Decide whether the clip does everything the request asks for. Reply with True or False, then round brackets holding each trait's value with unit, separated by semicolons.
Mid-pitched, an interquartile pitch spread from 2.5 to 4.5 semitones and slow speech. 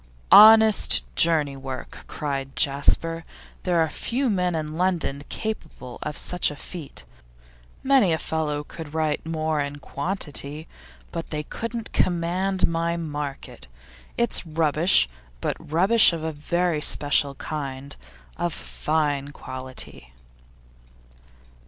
True (160 Hz; 3.5 semitones; 115 wpm)